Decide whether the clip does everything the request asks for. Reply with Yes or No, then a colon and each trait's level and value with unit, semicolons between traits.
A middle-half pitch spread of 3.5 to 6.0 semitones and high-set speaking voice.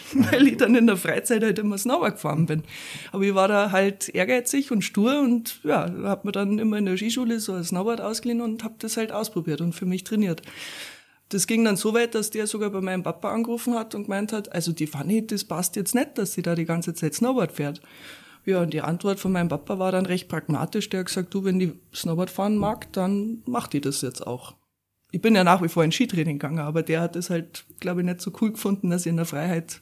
Yes: average, 4.4 semitones; high, 195 Hz